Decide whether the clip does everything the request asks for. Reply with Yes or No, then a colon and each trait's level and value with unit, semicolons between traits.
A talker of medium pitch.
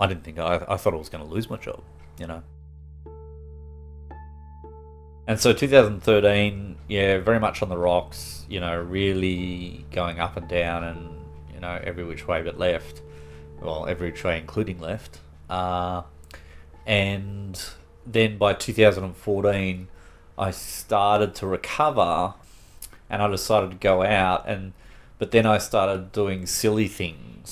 No: very low, 90 Hz